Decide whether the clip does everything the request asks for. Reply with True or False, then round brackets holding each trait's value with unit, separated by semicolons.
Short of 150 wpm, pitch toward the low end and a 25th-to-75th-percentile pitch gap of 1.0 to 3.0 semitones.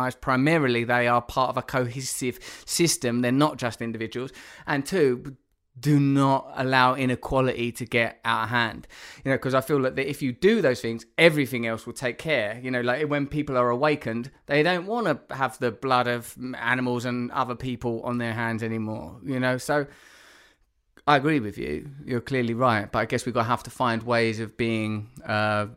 False (200 wpm; 125 Hz; 2.5 semitones)